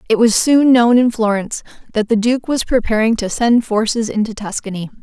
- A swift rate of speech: No, average, 190 wpm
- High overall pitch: Yes, high, 225 Hz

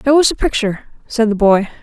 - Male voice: No, female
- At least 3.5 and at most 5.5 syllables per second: No, 6.4 syllables/s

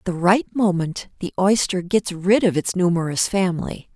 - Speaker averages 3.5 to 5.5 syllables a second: Yes, 4.9 syllables/s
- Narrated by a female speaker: Yes, female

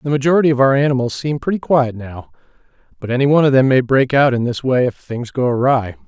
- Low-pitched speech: Yes, low, 130 Hz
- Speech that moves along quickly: Yes, fast, 235 wpm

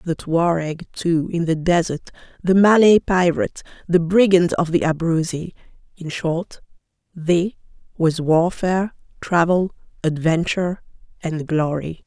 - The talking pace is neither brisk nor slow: No, slow, 110 wpm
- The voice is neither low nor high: Yes, medium, 170 Hz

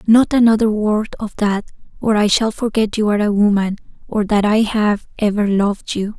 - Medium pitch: No, high, 210 Hz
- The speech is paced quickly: No, average, 195 wpm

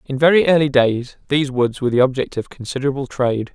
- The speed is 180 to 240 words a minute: Yes, fast, 205 wpm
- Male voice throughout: Yes, male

